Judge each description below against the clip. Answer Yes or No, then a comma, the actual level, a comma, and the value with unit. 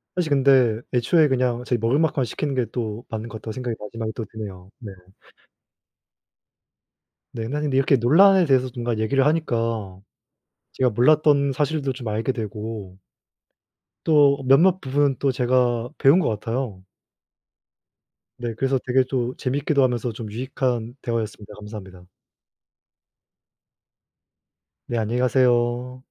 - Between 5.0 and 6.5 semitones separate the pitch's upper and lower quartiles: No, average, 3.3 semitones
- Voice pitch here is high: No, low, 125 Hz